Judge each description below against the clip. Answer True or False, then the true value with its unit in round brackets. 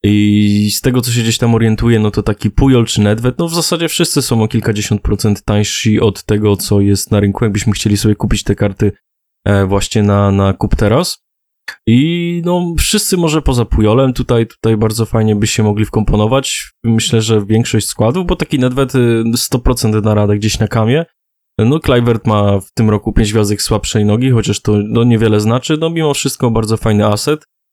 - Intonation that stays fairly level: False (3.1 semitones)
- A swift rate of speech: True (190 wpm)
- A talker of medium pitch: False (110 Hz)